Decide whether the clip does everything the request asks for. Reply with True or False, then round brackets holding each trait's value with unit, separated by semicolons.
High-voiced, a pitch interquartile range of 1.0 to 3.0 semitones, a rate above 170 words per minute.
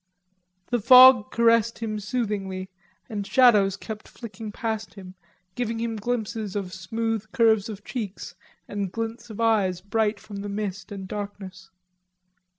False (215 Hz; 2.4 semitones; 140 wpm)